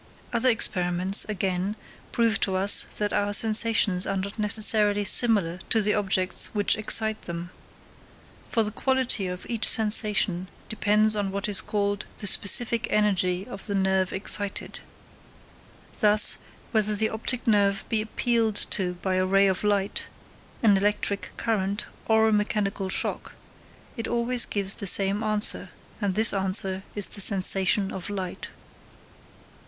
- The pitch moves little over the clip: Yes, narrow, 2.1 semitones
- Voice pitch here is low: No, high, 205 Hz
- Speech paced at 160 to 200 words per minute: No, average, 145 wpm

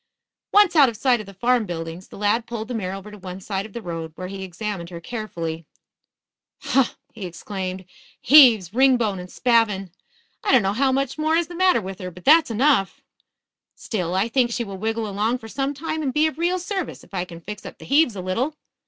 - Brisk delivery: Yes, fast, 220 wpm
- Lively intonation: Yes, wide, 5.9 semitones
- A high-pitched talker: Yes, high, 220 Hz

